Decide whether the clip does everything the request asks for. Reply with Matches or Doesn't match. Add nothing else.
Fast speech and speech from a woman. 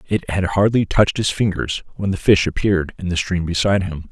Doesn't match